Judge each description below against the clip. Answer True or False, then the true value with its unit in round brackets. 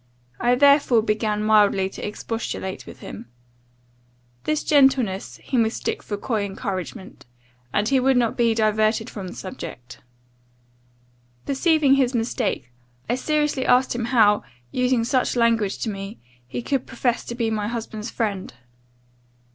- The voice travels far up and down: False (3.5 semitones)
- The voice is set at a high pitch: True (225 Hz)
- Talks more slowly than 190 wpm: True (140 wpm)